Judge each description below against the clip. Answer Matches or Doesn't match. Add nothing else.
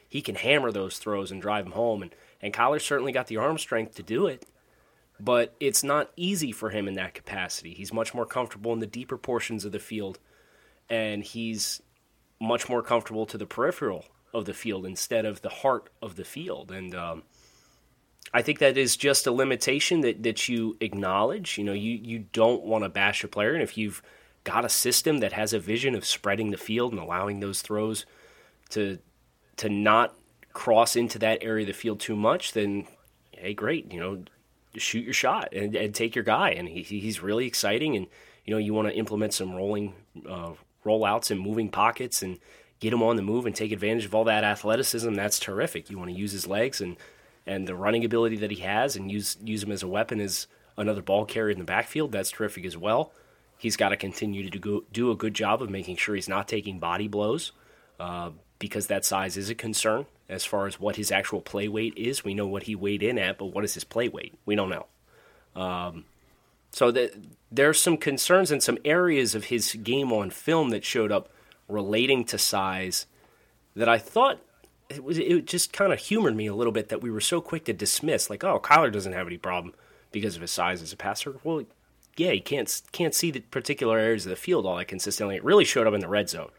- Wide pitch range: Doesn't match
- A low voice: Matches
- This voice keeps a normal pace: Doesn't match